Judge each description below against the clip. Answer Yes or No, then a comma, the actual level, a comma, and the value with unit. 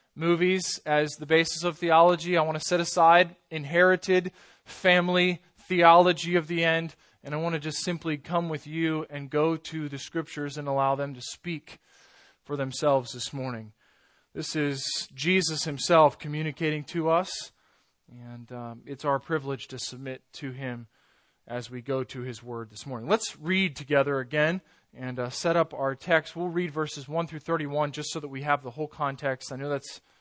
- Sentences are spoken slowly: No, average, 180 wpm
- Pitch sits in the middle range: Yes, medium, 155 Hz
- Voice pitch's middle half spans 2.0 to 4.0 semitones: Yes, average, 3.5 semitones